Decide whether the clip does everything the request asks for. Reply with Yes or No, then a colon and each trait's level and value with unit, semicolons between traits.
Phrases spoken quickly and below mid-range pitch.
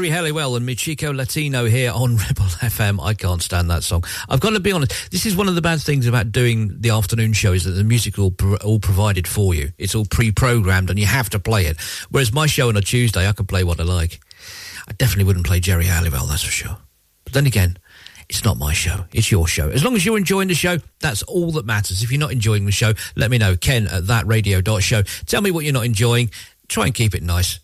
Yes: fast, 250 wpm; low, 110 Hz